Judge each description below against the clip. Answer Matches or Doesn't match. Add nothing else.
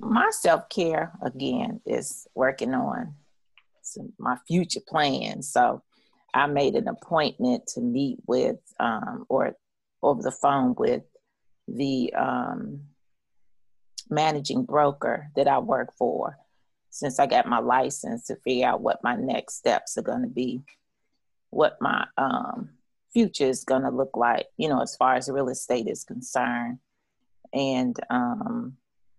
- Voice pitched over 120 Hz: Matches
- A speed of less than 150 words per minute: Matches